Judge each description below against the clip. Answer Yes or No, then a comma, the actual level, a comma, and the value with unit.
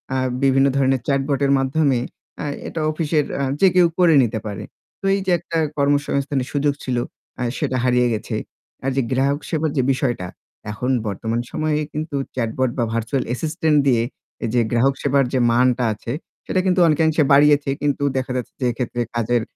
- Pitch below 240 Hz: Yes, low, 135 Hz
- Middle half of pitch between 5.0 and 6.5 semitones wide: No, average, 3.2 semitones